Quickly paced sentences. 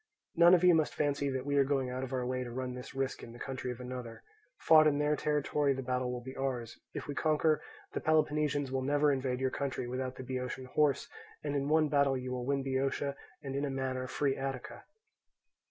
Yes: fast, 230 wpm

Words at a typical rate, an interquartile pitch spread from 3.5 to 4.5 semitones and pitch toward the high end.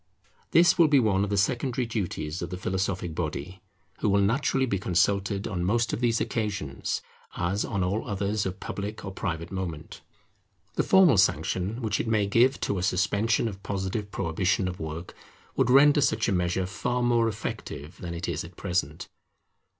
No: average, 180 wpm; average, 4.1 semitones; low, 100 Hz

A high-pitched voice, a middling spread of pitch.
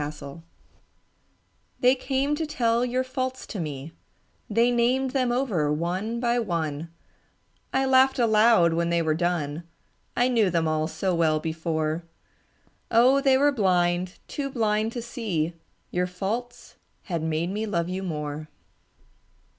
No: high, 200 Hz; wide, 6.8 semitones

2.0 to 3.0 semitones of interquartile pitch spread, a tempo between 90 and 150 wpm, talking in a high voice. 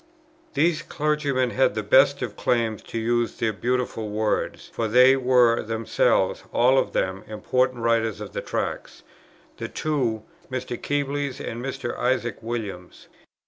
No: average, 2.7 semitones; average, 140 wpm; low, 120 Hz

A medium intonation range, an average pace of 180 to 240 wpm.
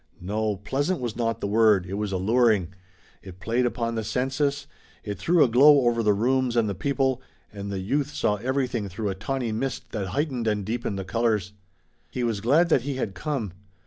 Yes: average, 4.5 semitones; average, 200 wpm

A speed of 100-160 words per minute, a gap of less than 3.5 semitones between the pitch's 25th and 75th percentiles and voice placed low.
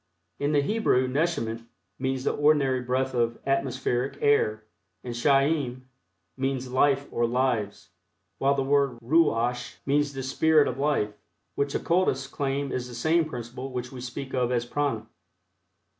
Yes: average, 145 wpm; narrow, 2.5 semitones; low, 130 Hz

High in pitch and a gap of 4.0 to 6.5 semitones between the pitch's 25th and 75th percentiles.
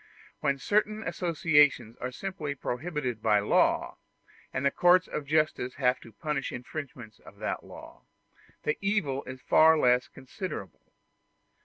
No: medium, 140 Hz; average, 4.8 semitones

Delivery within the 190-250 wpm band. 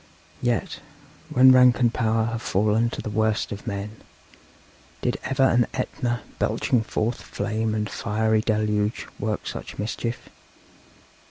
No: slow, 135 wpm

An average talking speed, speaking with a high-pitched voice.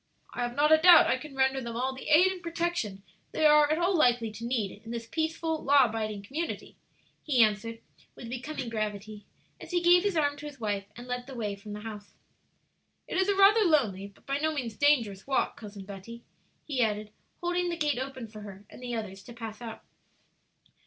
No: fast, 215 wpm; high, 245 Hz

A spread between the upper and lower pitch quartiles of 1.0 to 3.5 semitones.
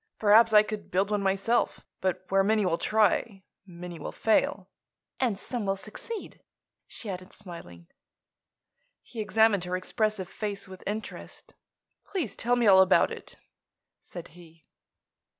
Yes: average, 2.9 semitones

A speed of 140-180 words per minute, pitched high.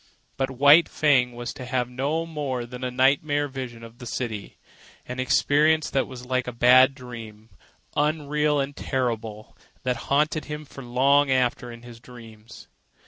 No: average, 155 wpm; low, 130 Hz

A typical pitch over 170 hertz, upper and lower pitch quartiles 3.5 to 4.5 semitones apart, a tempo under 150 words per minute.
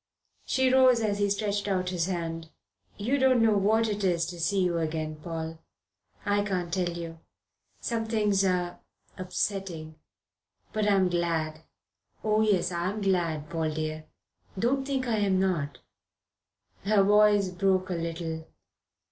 Yes: medium, 185 Hz; average, 3.8 semitones; average, 140 wpm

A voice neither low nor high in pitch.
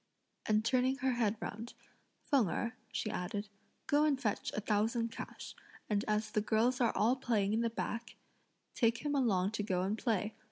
No: high, 225 Hz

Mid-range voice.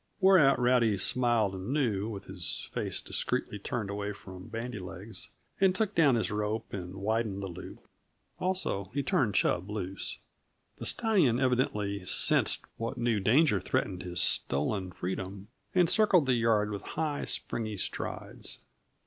No: low, 110 Hz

